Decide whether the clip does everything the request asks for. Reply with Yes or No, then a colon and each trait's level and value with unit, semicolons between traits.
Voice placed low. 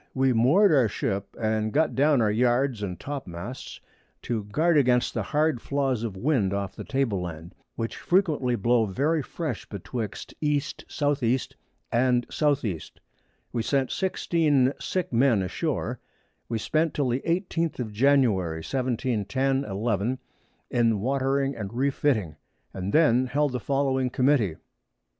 Yes: low, 125 Hz